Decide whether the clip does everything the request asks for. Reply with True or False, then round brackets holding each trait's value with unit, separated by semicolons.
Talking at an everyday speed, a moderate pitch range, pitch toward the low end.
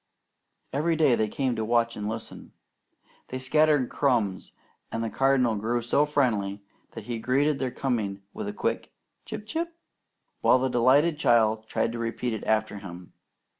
True (165 wpm; 3.9 semitones; 120 Hz)